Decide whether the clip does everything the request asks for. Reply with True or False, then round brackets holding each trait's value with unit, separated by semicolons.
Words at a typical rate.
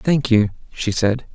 True (180 wpm)